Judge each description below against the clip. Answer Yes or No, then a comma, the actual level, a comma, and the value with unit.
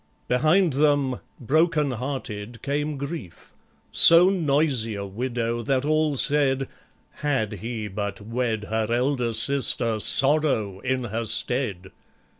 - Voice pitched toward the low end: Yes, low, 130 Hz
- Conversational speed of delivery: No, slow, 115 wpm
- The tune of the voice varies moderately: Yes, average, 4.6 semitones